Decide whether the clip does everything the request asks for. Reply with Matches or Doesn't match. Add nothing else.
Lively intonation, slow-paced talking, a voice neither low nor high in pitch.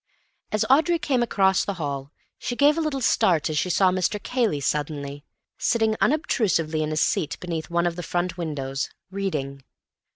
Doesn't match